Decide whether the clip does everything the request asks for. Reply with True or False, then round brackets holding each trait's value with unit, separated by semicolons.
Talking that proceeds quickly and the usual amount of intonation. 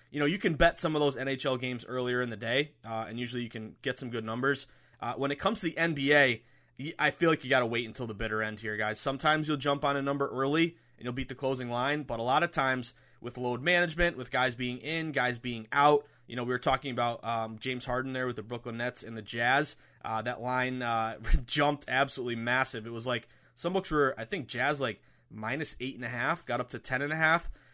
True (255 wpm; 3.2 semitones)